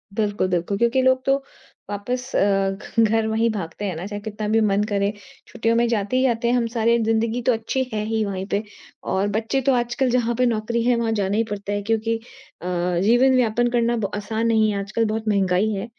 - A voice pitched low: No, high, 225 Hz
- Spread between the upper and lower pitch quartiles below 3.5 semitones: Yes, narrow, 2.5 semitones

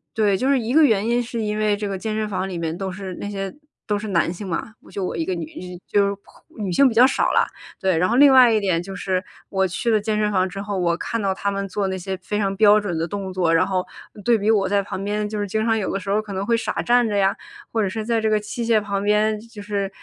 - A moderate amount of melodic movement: No, narrow, 2.3 semitones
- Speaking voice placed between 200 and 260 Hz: Yes, high, 205 Hz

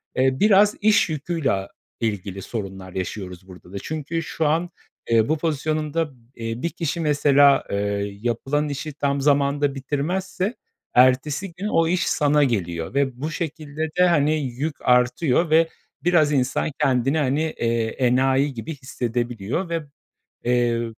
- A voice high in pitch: No, medium, 140 Hz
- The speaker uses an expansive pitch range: No, average, 4.7 semitones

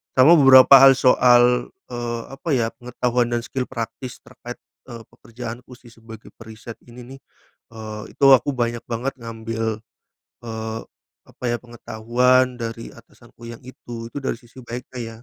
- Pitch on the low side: Yes, low, 120 Hz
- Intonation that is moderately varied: No, narrow, 1.7 semitones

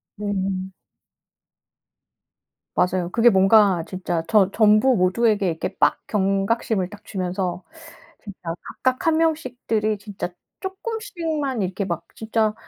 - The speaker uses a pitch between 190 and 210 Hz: Yes, high, 205 Hz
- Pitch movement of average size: Yes, average, 4.0 semitones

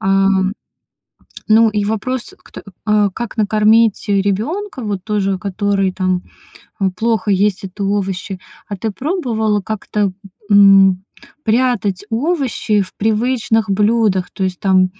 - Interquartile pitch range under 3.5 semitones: Yes, narrow, 2.5 semitones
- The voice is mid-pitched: No, high, 205 Hz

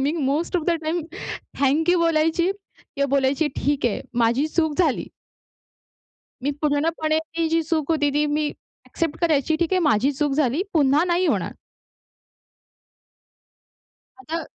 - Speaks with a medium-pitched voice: No, very high, 310 Hz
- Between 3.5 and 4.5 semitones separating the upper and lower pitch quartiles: No, average, 2.7 semitones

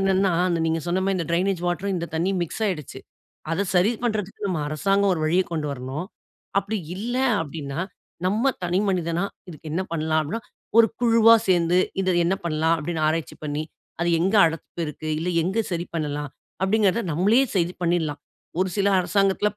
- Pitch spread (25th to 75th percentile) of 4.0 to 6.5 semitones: No, average, 3.4 semitones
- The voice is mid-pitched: Yes, medium, 175 Hz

